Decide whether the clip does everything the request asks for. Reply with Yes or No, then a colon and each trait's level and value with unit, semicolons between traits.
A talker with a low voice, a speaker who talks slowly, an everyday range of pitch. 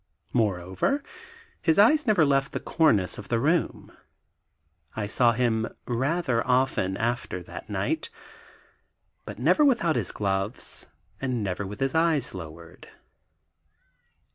No: low, 120 Hz; slow, 120 wpm; wide, 7.8 semitones